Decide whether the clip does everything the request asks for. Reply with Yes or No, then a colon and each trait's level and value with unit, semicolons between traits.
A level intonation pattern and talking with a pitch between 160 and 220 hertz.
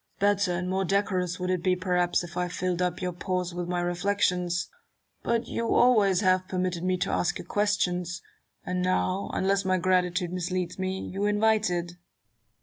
Yes: narrow, 1.5 semitones; medium, 185 Hz